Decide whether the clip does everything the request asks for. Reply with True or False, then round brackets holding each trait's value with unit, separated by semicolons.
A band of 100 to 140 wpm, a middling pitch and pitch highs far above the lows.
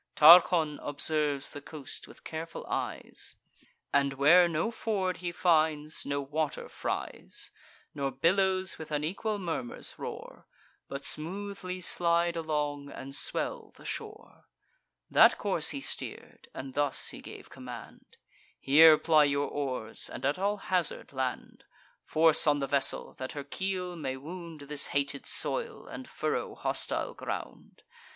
False (135 wpm; 155 Hz; 3.7 semitones)